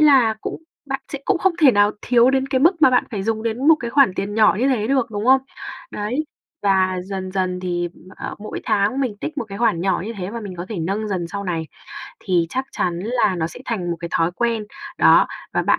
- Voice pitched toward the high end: Yes, high, 215 Hz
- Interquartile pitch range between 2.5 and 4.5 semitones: No, wide, 5.4 semitones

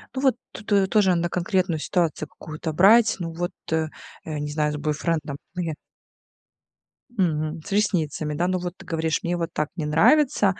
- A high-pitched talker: No, medium, 170 Hz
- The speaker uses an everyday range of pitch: Yes, average, 3.2 semitones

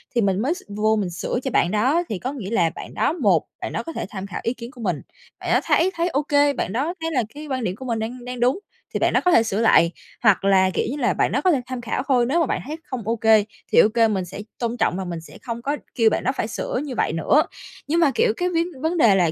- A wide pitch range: Yes, wide, 6.0 semitones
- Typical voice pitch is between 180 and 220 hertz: No, high, 240 Hz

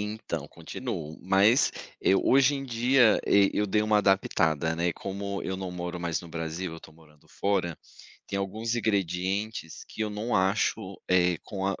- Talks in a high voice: No, very low, 95 Hz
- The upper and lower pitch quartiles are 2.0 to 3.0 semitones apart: No, average, 3.5 semitones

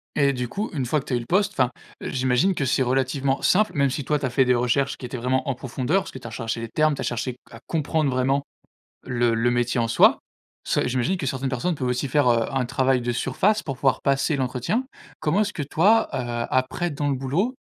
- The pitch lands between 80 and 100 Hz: No, low, 130 Hz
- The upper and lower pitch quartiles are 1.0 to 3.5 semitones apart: Yes, average, 3.2 semitones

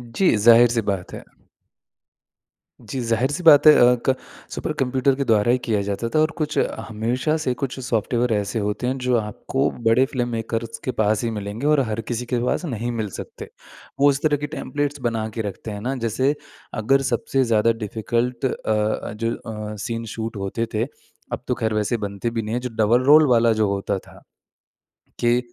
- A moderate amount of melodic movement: Yes, average, 3.1 semitones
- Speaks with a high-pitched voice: No, low, 115 Hz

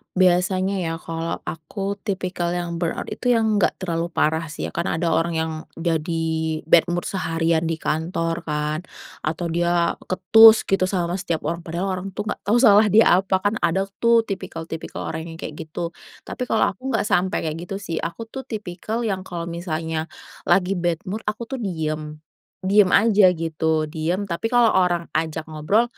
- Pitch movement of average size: Yes, average, 3.3 semitones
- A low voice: No, medium, 175 Hz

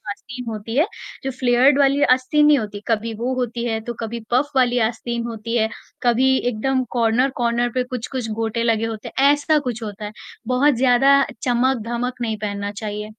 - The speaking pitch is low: No, high, 240 Hz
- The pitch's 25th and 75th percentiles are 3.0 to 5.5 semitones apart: No, narrow, 2.6 semitones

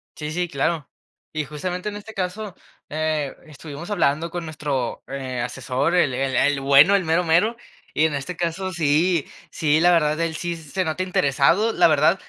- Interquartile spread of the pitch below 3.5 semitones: No, average, 3.8 semitones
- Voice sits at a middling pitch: Yes, medium, 160 Hz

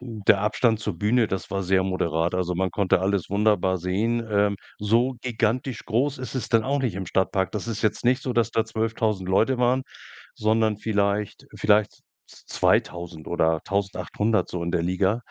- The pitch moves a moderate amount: Yes, average, 3.3 semitones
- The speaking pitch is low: Yes, low, 105 Hz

